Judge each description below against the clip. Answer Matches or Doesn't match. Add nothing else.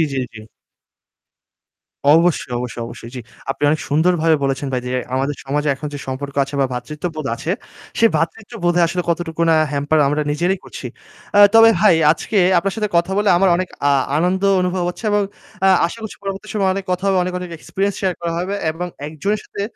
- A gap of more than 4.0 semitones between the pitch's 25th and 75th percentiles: Matches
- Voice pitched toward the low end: Doesn't match